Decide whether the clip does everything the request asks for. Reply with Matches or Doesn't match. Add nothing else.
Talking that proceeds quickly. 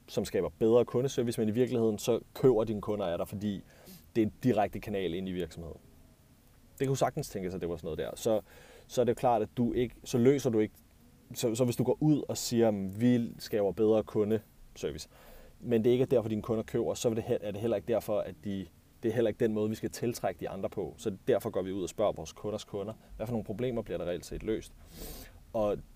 Matches